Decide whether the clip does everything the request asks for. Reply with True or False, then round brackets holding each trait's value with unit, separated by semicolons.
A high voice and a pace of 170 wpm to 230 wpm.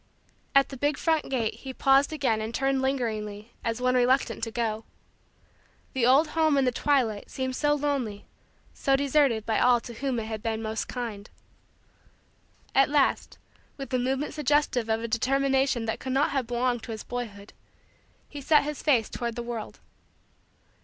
True (255 Hz; 175 wpm)